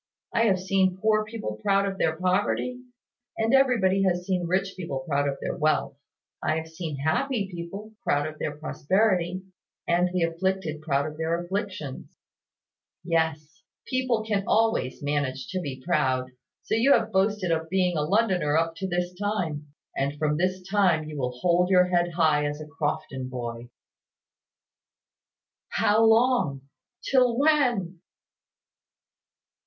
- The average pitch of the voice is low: No, medium, 180 Hz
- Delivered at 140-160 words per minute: Yes, average, 150 wpm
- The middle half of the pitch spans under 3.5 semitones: No, average, 4.6 semitones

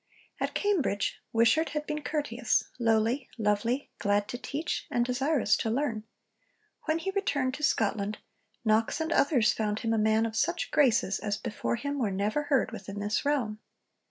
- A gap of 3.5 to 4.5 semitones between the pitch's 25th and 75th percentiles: No, average, 5.2 semitones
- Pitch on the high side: Yes, high, 235 Hz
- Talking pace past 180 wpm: No, average, 165 wpm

